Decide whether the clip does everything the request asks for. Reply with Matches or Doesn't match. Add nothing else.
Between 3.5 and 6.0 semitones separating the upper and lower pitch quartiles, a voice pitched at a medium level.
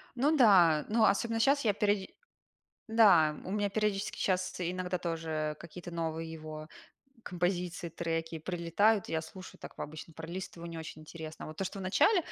Matches